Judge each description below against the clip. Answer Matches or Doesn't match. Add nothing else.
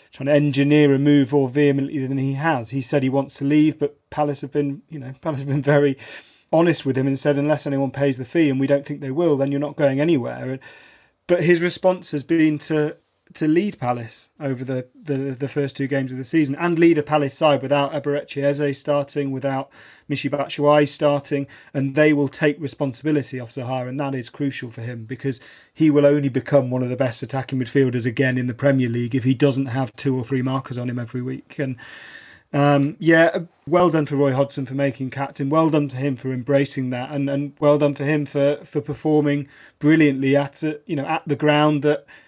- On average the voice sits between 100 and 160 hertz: Matches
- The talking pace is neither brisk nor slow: Doesn't match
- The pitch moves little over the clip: Matches